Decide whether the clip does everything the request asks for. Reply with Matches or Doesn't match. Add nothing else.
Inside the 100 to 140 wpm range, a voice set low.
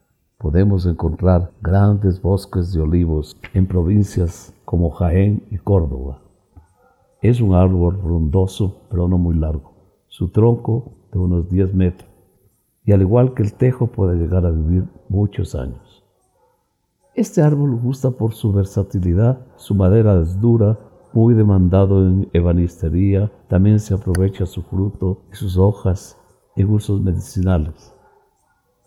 Matches